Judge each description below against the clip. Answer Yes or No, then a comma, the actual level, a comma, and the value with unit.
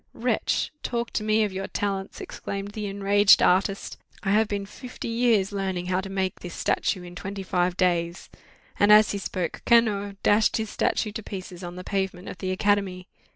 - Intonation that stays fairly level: Yes, narrow, 2.0 semitones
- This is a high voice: Yes, high, 195 Hz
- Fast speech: No, average, 185 wpm